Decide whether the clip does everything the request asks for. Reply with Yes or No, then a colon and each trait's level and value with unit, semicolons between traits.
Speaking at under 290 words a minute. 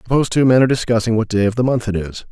No: fast, 310 wpm